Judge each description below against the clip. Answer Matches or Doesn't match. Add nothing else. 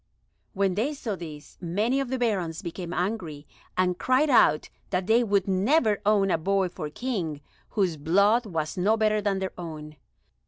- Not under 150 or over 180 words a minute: Matches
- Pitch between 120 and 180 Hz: Doesn't match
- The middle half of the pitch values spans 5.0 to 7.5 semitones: Doesn't match